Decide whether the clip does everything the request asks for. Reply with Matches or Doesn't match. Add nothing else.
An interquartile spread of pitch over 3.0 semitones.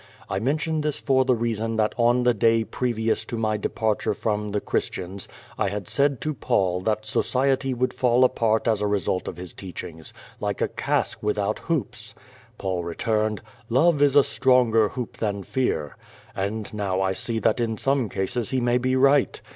Matches